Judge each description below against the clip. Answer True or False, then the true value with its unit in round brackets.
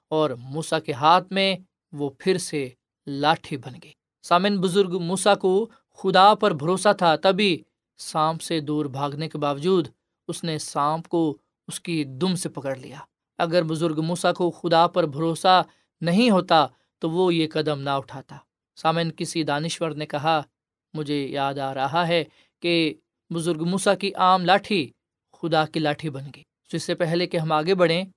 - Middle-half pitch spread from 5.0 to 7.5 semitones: False (3.2 semitones)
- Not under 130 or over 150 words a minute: False (170 wpm)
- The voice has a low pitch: False (165 Hz)